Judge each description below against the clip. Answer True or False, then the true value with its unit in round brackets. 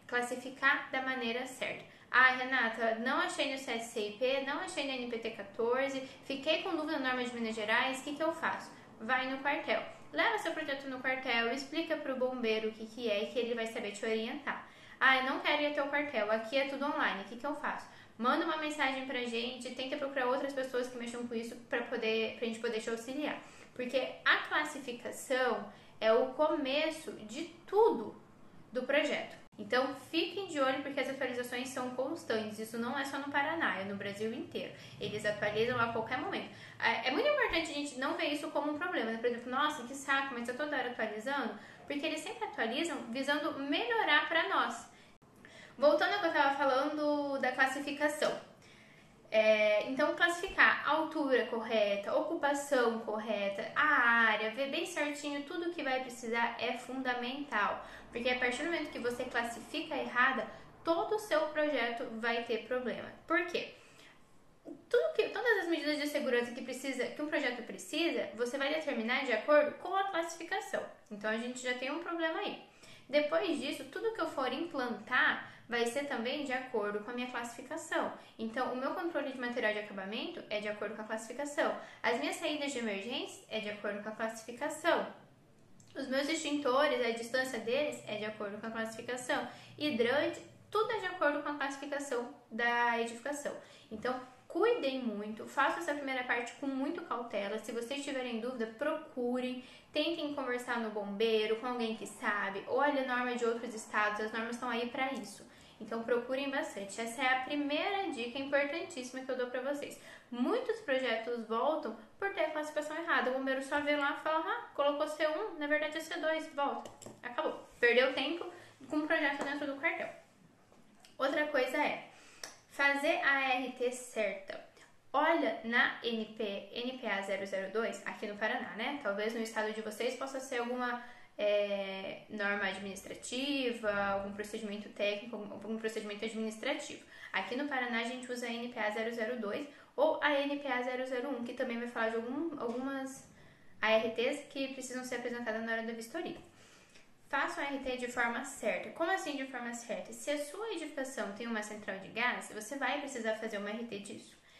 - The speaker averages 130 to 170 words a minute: False (180 wpm)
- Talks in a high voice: True (260 Hz)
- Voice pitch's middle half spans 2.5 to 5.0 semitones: True (4.1 semitones)